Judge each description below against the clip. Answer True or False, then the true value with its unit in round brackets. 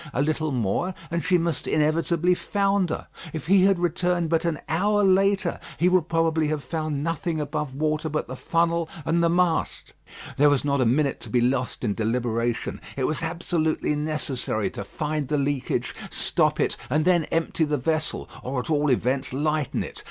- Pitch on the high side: False (155 Hz)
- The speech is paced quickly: False (180 wpm)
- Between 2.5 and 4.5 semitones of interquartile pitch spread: True (3.2 semitones)